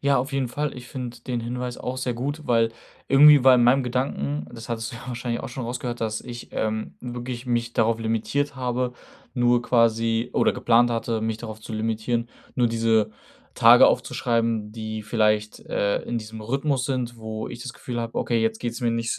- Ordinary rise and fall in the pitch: No, narrow, 1.8 semitones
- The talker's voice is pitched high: No, low, 120 Hz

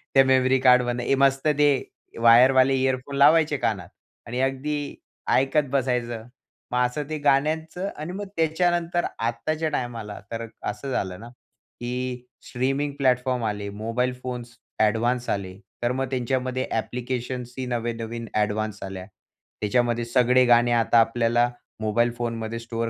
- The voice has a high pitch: No, low, 125 Hz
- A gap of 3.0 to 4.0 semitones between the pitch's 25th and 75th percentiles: No, narrow, 2.5 semitones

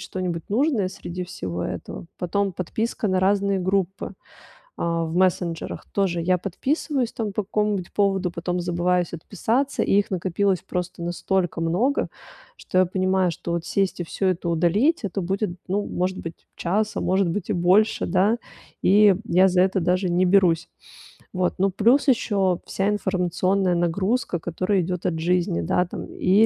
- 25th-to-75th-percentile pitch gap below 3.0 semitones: Yes, narrow, 2.4 semitones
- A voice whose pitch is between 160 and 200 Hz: Yes, medium, 185 Hz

